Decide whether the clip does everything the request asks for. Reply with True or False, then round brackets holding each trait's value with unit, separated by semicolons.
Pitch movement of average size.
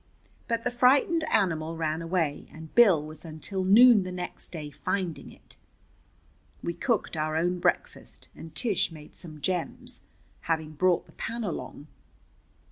True (4.8 semitones)